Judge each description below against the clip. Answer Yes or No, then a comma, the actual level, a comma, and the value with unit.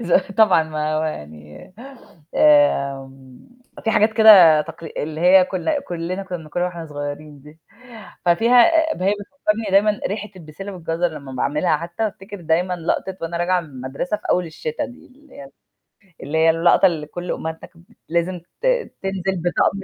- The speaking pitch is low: No, medium, 175 Hz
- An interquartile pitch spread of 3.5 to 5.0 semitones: Yes, average, 4.1 semitones